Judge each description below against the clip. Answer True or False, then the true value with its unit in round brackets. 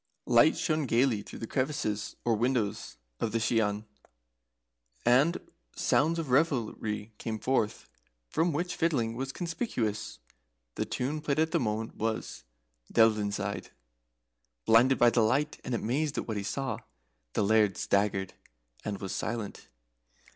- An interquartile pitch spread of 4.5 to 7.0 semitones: True (4.8 semitones)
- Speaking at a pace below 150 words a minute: True (140 wpm)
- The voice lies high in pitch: False (115 Hz)